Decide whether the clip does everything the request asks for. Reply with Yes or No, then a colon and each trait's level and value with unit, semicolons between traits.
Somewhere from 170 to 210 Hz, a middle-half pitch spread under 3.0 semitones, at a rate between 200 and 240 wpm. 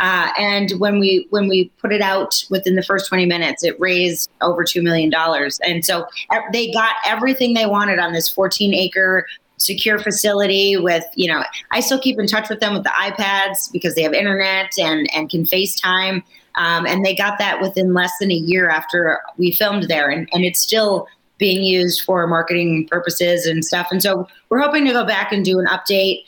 Yes: high, 190 Hz; narrow, 2.5 semitones; fast, 205 wpm